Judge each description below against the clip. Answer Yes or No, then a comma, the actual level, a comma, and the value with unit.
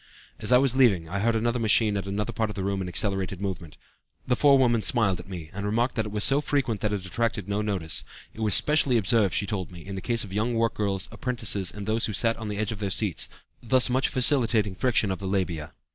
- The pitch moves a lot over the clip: No, average, 3.3 semitones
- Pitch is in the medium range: No, low, 105 Hz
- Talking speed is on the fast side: Yes, fast, 250 wpm